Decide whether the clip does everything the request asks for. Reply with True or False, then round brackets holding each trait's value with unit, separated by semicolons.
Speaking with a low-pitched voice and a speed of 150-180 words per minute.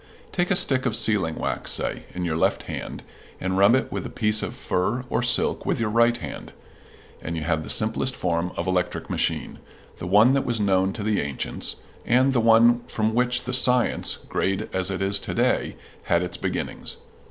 False (105 Hz; 200 wpm)